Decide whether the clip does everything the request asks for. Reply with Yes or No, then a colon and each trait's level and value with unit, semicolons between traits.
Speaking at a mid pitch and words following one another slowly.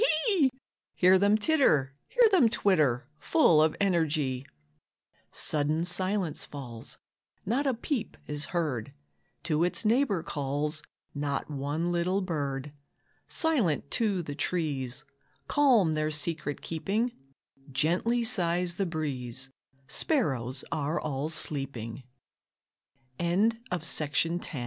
Yes: medium, 165 Hz; slow, 90 wpm